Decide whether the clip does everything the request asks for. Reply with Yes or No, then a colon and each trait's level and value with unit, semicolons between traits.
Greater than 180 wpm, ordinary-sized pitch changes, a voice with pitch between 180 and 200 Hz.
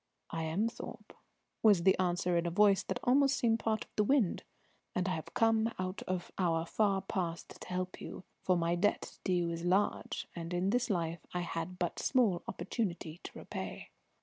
Yes: average, 195 wpm; average, 3.6 semitones; medium, 185 Hz